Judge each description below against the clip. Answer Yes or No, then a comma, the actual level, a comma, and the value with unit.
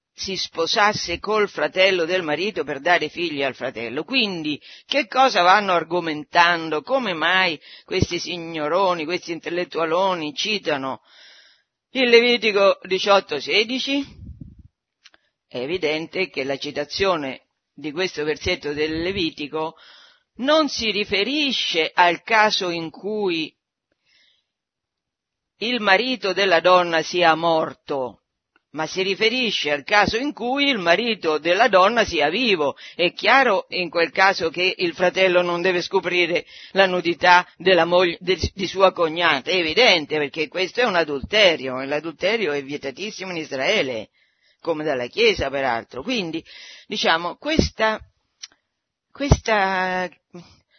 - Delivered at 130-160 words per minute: No, average, 120 wpm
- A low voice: No, medium, 180 Hz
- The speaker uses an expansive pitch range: No, average, 4.2 semitones